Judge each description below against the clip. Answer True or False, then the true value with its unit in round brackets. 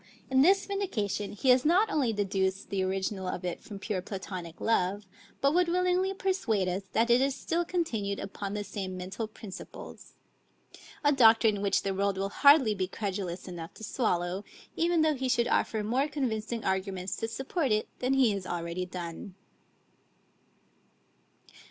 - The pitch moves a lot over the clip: True (5.9 semitones)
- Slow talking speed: False (165 wpm)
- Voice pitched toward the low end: False (210 Hz)